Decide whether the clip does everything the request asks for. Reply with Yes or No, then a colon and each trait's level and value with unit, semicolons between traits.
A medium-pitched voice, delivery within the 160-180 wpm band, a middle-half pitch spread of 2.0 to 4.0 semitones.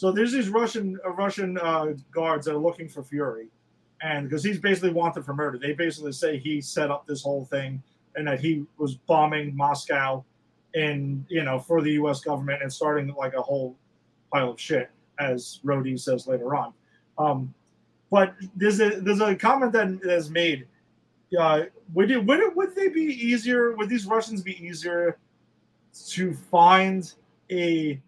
No: medium, 160 Hz; average, 175 wpm; average, 5.3 semitones